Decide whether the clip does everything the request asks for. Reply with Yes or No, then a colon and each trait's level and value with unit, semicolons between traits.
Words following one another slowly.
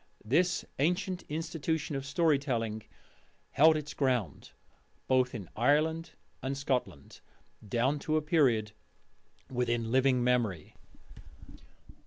Yes: slow, 105 wpm